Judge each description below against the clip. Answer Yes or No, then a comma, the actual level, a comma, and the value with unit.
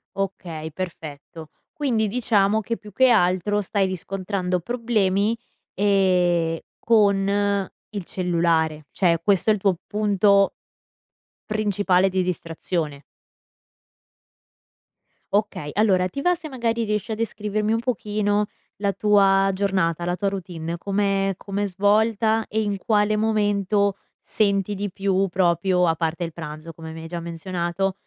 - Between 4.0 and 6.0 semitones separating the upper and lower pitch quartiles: No, average, 2.9 semitones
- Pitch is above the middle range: Yes, high, 195 Hz